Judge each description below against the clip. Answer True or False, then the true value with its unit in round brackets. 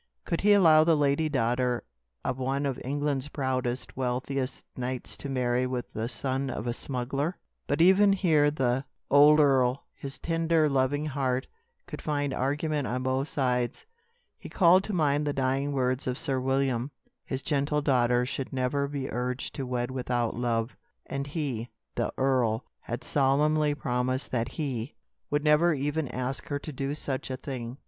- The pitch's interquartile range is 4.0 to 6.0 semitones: False (2.6 semitones)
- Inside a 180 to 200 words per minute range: False (165 wpm)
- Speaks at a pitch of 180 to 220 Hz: False (135 Hz)